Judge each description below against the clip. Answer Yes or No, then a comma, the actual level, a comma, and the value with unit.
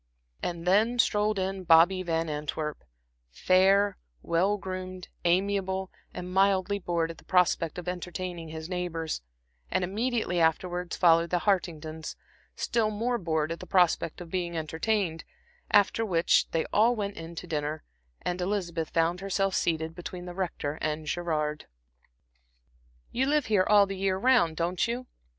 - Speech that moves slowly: No, average, 150 wpm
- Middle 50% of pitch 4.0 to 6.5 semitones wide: No, average, 3.0 semitones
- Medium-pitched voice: Yes, medium, 180 Hz